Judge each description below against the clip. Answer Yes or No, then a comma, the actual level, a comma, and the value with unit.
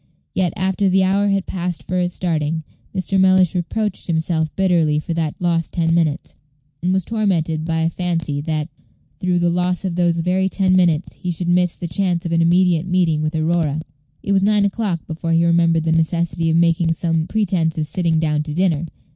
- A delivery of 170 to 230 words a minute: Yes, average, 195 wpm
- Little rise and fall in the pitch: Yes, narrow, 2.2 semitones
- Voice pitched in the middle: Yes, medium, 170 Hz